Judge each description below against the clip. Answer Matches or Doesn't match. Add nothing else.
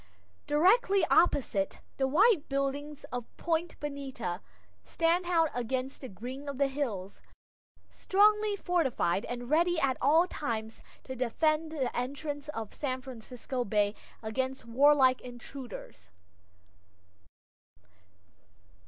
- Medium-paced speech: Doesn't match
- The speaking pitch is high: Matches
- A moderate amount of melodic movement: Matches